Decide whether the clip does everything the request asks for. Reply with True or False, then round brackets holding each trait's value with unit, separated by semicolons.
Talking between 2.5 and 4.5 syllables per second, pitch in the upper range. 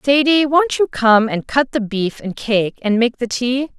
True (4.2 syllables/s; 245 Hz)